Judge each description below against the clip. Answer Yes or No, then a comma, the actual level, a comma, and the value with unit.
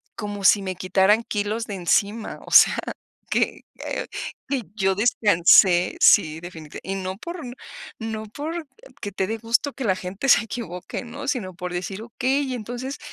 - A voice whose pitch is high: Yes, high, 210 Hz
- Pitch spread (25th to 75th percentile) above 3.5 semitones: Yes, average, 4.5 semitones